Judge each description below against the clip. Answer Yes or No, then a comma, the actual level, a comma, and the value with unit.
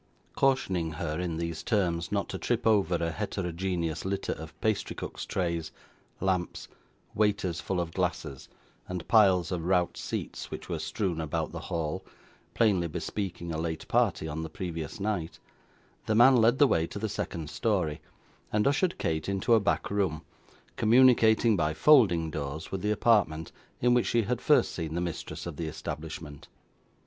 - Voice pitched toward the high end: No, very low, 90 Hz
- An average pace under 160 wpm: No, average, 165 wpm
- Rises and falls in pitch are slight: No, average, 4.6 semitones